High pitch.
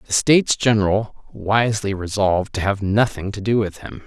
No: low, 105 Hz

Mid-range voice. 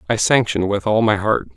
No: low, 110 Hz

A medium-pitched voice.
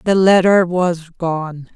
Yes: medium, 175 Hz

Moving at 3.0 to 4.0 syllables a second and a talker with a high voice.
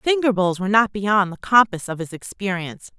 No: 5.6 syllables/s; high, 200 Hz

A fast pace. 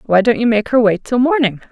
Yes: fast, 280 wpm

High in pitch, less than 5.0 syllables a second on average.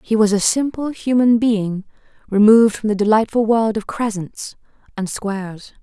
Yes: high, 215 Hz; 4.8 syllables/s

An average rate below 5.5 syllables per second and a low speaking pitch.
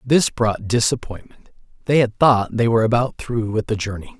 Yes: 5.1 syllables/s; low, 115 Hz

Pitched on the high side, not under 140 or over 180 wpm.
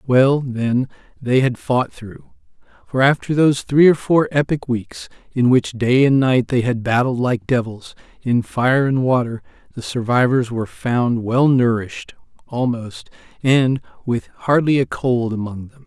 No: low, 125 Hz; average, 160 wpm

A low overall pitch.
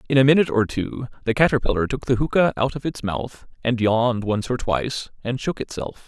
Yes: low, 120 Hz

